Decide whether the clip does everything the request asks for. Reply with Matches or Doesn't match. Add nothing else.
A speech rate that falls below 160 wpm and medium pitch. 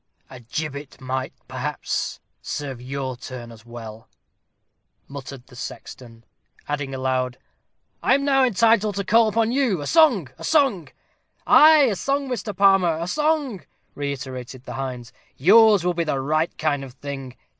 Matches